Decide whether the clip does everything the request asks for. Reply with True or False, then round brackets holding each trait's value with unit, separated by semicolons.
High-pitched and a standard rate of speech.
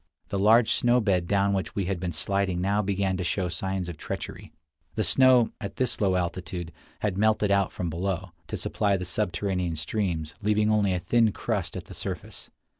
False (95 Hz; 190 wpm)